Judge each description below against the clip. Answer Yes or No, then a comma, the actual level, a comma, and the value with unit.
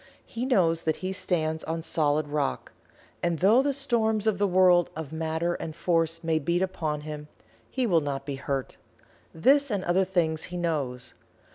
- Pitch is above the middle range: No, medium, 165 Hz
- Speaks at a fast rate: No, average, 175 wpm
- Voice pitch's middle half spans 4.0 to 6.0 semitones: No, average, 3.4 semitones